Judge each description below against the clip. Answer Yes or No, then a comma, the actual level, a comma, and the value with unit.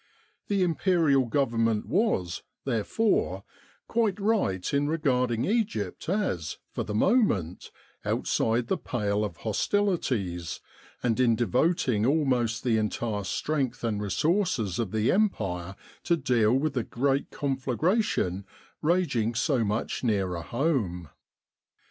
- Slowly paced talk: Yes, slow, 115 wpm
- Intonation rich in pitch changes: Yes, wide, 7.3 semitones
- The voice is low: Yes, low, 125 Hz